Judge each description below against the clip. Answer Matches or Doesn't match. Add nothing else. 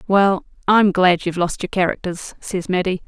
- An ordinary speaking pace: Matches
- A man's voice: Doesn't match